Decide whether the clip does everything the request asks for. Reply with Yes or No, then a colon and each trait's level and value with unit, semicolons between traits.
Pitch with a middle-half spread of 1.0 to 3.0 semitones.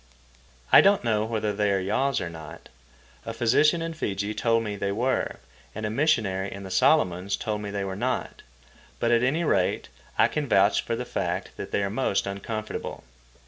No: average, 3.6 semitones